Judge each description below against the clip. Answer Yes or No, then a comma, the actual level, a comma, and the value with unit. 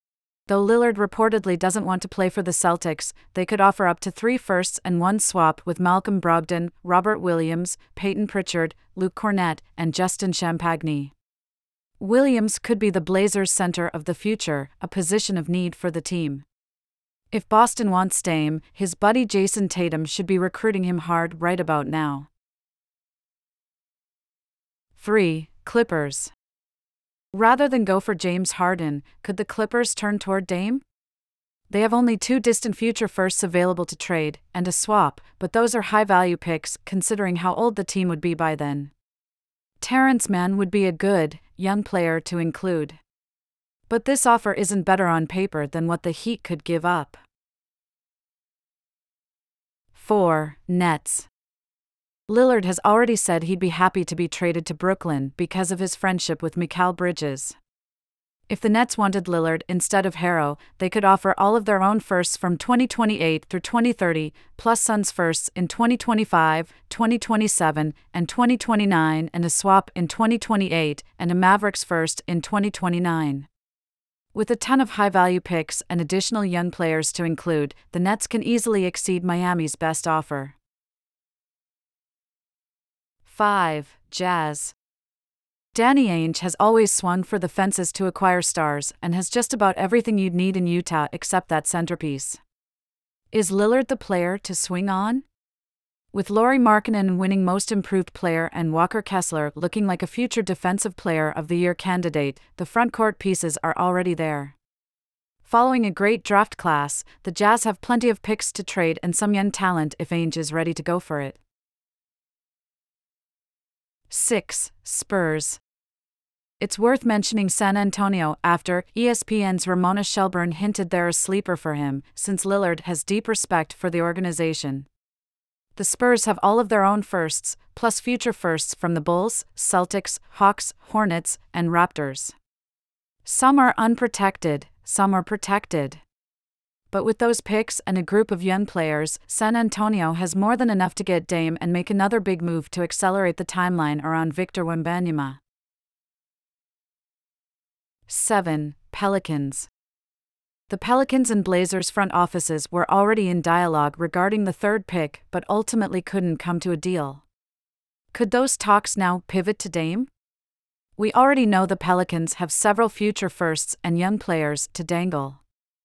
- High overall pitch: No, medium, 180 Hz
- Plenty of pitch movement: No, average, 3.9 semitones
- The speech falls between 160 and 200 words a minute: No, average, 150 wpm